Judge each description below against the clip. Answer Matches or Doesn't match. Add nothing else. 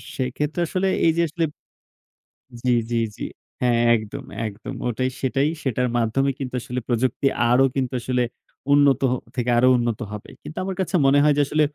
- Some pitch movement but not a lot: Matches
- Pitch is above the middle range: Doesn't match